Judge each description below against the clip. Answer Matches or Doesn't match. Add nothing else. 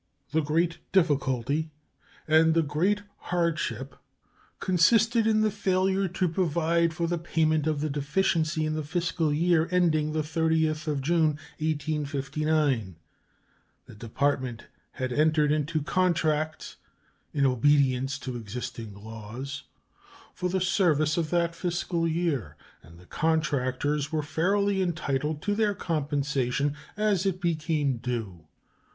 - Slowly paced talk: Matches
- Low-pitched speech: Doesn't match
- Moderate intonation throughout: Matches